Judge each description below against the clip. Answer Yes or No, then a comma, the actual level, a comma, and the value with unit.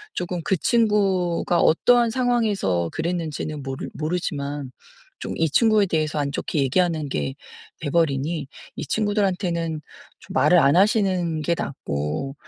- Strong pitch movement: No, average, 5.0 semitones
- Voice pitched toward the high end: No, medium, 170 Hz